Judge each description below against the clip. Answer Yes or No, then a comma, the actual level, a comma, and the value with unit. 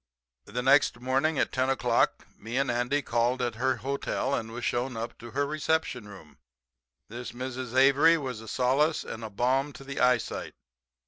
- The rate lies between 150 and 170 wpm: No, average, 180 wpm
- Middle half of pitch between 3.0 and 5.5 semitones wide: No, narrow, 2.4 semitones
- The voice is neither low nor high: No, low, 130 Hz